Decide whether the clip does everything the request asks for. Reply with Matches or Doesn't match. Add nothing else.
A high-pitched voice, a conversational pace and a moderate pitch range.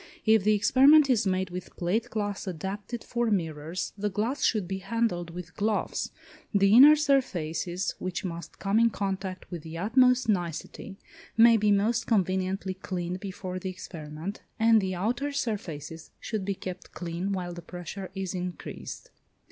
Matches